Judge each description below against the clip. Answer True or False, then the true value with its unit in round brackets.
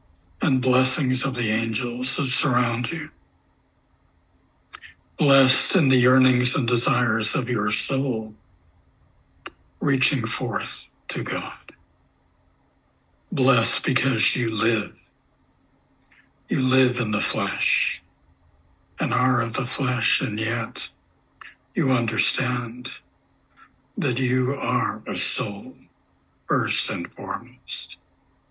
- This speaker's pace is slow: True (100 wpm)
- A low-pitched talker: True (120 Hz)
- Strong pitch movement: True (6.7 semitones)